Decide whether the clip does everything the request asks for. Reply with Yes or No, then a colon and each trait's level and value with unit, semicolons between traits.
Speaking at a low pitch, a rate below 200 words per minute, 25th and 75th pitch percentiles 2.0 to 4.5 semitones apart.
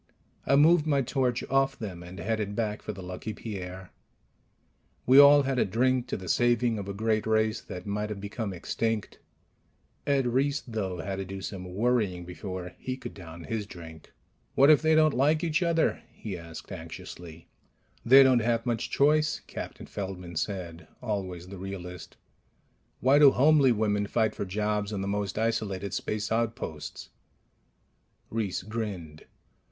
No: low, 105 Hz; average, 160 wpm; average, 5.0 semitones